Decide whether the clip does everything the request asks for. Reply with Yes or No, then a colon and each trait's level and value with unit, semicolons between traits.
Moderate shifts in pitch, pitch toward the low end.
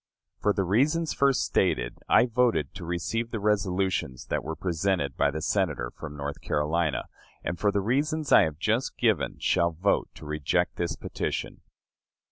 No: wide, 6.1 semitones; very low, 90 Hz